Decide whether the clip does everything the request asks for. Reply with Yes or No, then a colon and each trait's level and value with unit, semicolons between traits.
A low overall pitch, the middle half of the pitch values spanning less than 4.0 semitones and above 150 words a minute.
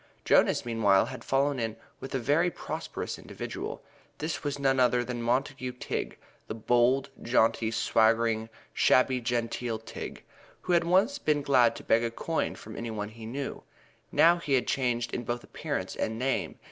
Yes: low, 120 Hz; average, 3.1 semitones; average, 170 wpm